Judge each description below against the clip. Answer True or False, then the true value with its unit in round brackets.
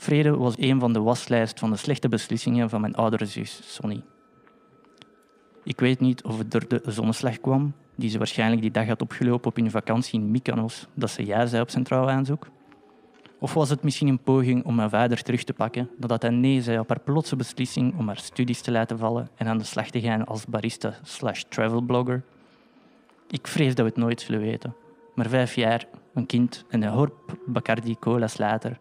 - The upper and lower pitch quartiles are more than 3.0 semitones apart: False (2.7 semitones)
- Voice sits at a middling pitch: False (120 Hz)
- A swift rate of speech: True (205 wpm)